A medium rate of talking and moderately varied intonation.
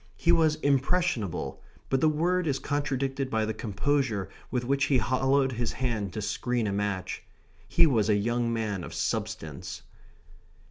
Yes: average, 155 wpm; average, 4.7 semitones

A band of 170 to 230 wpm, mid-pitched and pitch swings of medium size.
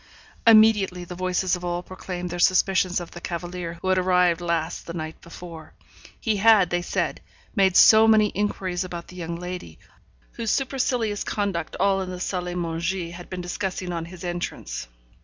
No: average, 175 wpm; medium, 180 Hz; narrow, 1.8 semitones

